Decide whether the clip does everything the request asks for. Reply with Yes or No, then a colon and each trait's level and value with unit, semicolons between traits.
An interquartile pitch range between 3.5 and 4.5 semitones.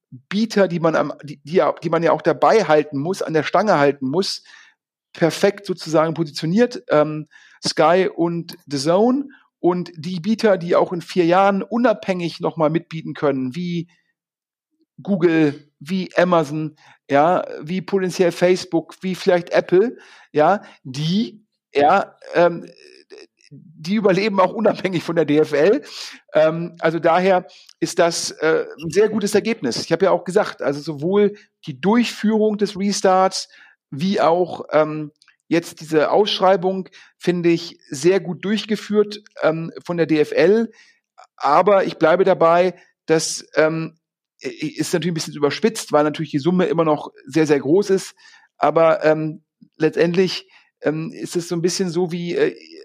Yes: average, 3.9 semitones